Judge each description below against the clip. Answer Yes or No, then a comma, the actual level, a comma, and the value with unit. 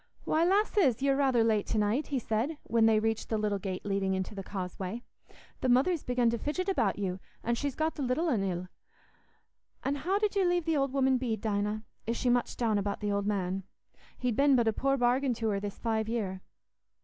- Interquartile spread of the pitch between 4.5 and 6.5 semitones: Yes, average, 5.0 semitones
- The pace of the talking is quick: Yes, fast, 220 wpm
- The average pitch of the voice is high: Yes, high, 235 Hz